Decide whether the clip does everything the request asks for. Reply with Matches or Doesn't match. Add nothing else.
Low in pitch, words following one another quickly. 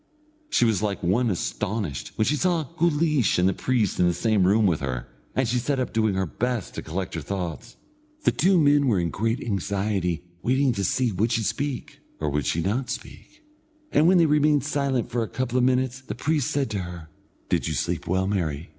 Matches